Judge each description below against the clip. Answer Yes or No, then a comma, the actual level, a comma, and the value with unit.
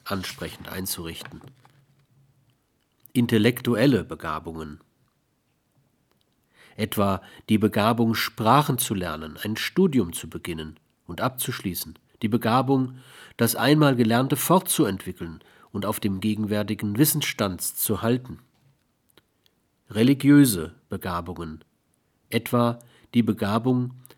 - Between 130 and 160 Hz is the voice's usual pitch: No, low, 115 Hz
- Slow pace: Yes, slow, 85 wpm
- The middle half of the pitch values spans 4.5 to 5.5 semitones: Yes, average, 5.1 semitones